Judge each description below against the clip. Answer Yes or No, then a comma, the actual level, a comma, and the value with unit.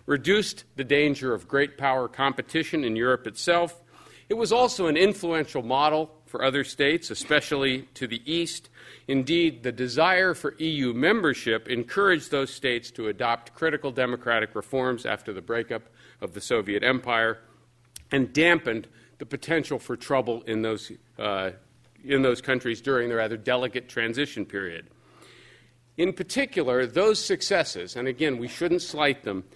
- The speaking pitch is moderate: No, low, 130 Hz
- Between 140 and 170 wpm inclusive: Yes, average, 145 wpm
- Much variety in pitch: No, average, 4.5 semitones